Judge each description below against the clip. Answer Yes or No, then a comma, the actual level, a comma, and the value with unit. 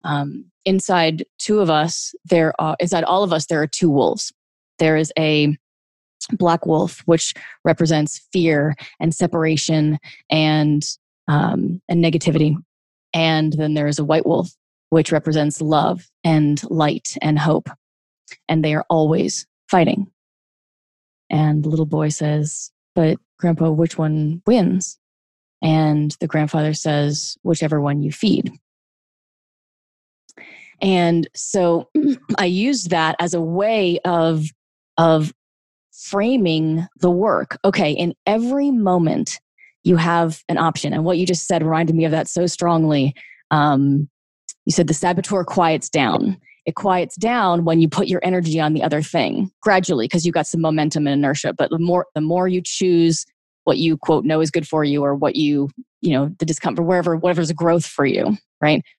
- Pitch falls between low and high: Yes, medium, 165 Hz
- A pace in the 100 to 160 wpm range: Yes, average, 155 wpm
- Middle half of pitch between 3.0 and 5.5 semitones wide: No, narrow, 2.6 semitones